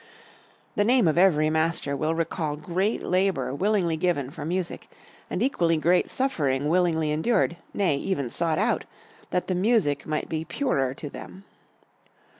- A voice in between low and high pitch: Yes, medium, 165 Hz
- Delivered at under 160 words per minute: Yes, average, 150 wpm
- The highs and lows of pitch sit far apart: No, average, 3.8 semitones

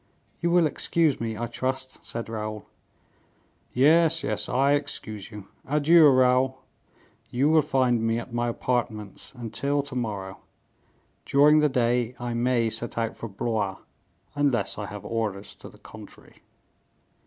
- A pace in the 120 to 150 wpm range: Yes, average, 145 wpm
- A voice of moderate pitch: No, low, 120 Hz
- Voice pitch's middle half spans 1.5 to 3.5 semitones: No, average, 4.0 semitones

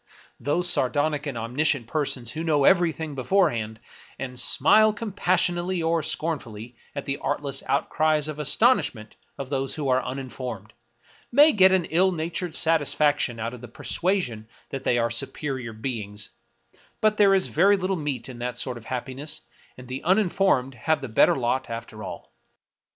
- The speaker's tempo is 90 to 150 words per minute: No, average, 160 wpm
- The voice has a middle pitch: Yes, medium, 145 Hz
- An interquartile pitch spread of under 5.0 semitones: No, wide, 5.6 semitones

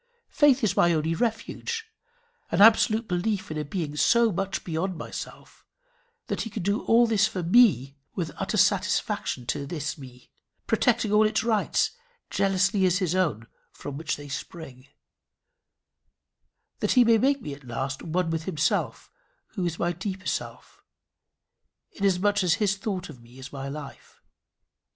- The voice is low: No, medium, 185 Hz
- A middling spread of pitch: No, wide, 6.0 semitones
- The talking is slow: No, average, 155 wpm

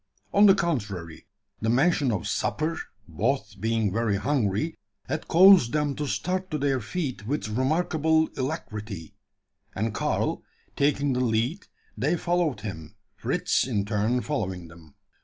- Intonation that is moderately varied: No, wide, 6.7 semitones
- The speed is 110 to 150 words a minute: Yes, average, 140 wpm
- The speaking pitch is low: Yes, low, 125 Hz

